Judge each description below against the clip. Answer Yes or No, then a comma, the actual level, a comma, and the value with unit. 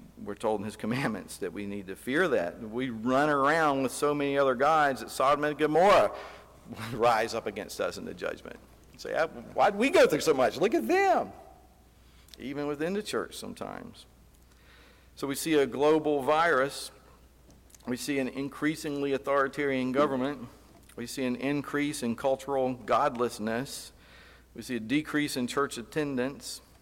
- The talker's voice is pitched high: No, low, 135 Hz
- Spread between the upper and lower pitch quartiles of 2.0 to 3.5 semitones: Yes, average, 3.2 semitones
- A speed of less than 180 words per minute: Yes, average, 165 wpm